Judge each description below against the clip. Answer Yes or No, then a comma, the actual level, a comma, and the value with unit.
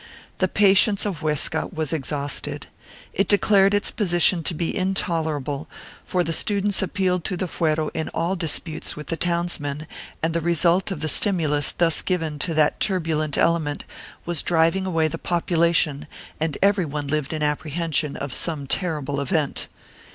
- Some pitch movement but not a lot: Yes, average, 3.2 semitones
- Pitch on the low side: No, medium, 165 Hz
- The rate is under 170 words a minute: Yes, average, 160 wpm